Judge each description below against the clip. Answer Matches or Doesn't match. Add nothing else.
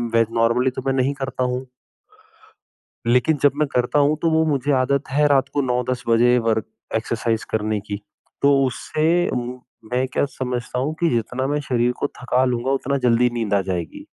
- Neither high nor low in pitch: Doesn't match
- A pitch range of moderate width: Matches